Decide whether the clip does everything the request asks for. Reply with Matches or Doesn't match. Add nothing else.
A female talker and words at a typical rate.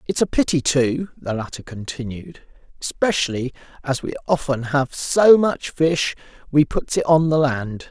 Doesn't match